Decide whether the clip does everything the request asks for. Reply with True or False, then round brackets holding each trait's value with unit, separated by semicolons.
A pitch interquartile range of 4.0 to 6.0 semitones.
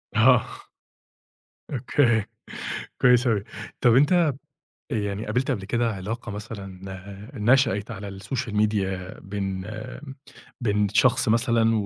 False (3.4 semitones)